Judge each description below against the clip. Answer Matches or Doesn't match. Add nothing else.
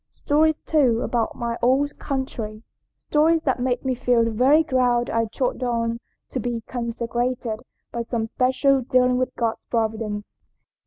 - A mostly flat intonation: Matches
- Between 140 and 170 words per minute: Matches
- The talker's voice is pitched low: Doesn't match